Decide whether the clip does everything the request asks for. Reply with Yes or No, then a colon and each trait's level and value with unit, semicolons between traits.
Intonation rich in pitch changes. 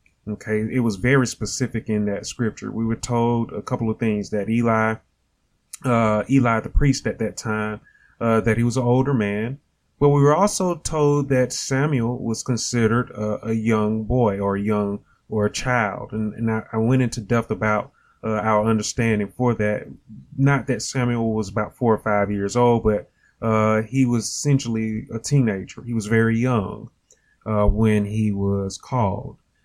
No: narrow, 2.5 semitones